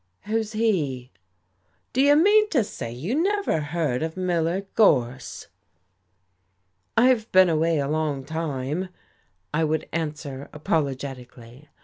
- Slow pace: Yes, slow, 115 wpm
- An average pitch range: No, wide, 7.3 semitones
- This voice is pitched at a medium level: Yes, medium, 160 Hz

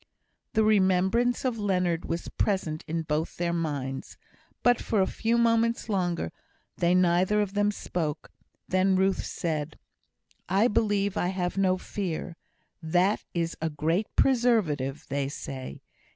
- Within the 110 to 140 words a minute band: Yes, slow, 135 wpm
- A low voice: No, medium, 185 Hz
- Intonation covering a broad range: No, average, 4.1 semitones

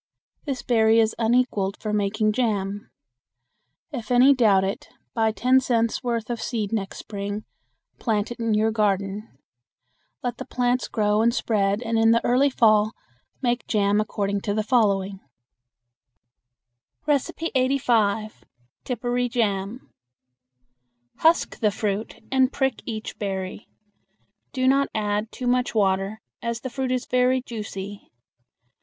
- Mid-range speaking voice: No, high, 225 Hz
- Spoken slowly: Yes, slow, 130 wpm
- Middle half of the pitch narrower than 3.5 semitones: Yes, average, 3.1 semitones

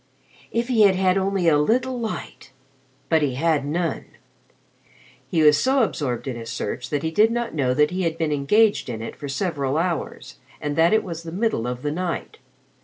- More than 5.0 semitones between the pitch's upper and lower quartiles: Yes, wide, 5.4 semitones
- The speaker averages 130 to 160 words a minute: No, average, 195 wpm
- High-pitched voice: No, medium, 165 Hz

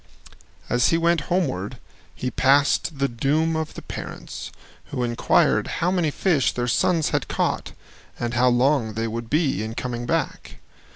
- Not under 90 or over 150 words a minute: No, average, 160 wpm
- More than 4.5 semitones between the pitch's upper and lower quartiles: Yes, average, 4.9 semitones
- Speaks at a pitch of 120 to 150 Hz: Yes, low, 135 Hz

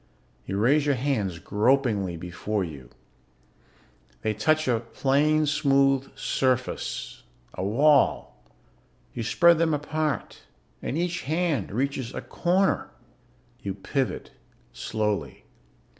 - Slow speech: Yes, slow, 105 wpm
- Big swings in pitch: Yes, wide, 6.3 semitones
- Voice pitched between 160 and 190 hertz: No, low, 135 Hz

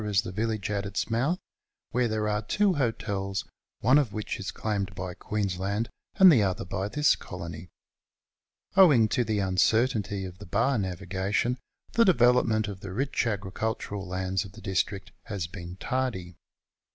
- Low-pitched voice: Yes, low, 105 Hz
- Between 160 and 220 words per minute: Yes, average, 165 wpm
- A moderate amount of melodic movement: Yes, average, 3.4 semitones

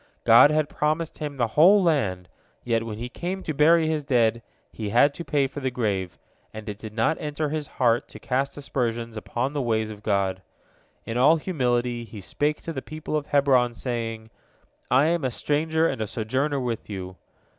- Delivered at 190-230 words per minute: Yes, average, 195 wpm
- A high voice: No, low, 125 Hz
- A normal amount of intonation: Yes, average, 5.0 semitones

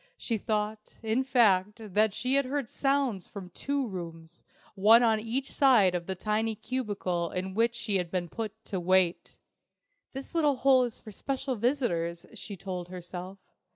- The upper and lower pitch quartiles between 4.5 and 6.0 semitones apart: Yes, average, 5.1 semitones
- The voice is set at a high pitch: Yes, high, 215 Hz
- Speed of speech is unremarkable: Yes, average, 160 wpm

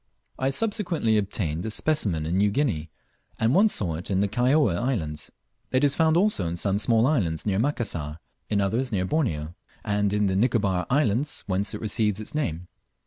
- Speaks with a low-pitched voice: Yes, low, 105 Hz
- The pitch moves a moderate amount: No, wide, 6.4 semitones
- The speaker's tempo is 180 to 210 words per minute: Yes, average, 185 wpm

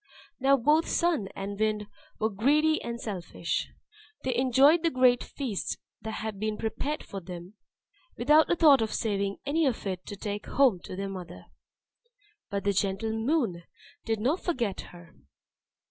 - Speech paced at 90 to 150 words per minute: No, average, 160 wpm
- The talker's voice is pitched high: Yes, high, 220 Hz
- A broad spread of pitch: Yes, wide, 5.7 semitones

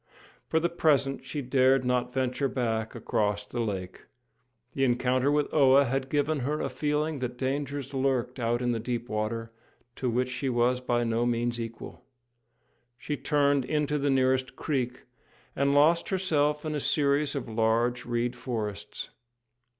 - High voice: No, low, 130 Hz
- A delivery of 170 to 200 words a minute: No, average, 160 wpm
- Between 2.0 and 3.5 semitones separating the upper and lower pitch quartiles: Yes, average, 3.0 semitones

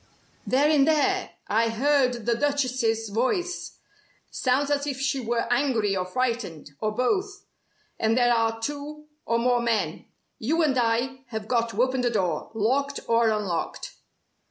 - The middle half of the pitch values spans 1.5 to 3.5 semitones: No, average, 3.9 semitones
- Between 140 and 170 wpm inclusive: Yes, average, 155 wpm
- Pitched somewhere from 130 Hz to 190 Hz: No, high, 245 Hz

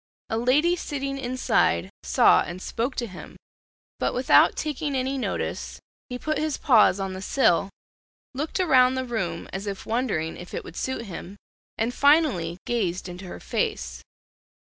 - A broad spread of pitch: Yes, wide, 6.4 semitones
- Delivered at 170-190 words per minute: No, average, 160 wpm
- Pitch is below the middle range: No, high, 245 Hz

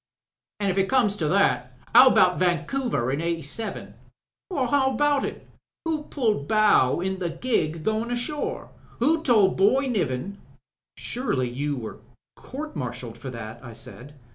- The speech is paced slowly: No, average, 150 wpm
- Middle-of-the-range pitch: No, high, 195 Hz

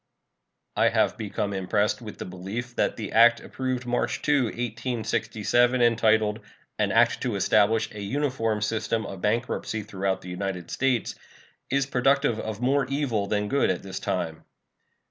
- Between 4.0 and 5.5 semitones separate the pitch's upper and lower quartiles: No, average, 3.2 semitones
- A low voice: Yes, low, 110 Hz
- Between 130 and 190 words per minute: Yes, average, 150 wpm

